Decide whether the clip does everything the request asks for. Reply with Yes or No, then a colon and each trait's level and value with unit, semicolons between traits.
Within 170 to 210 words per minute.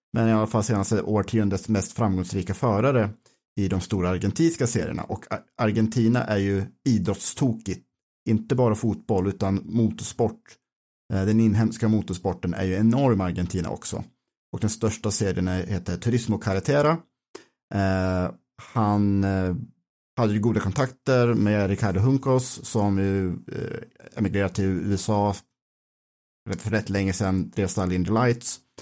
No: slow, 125 wpm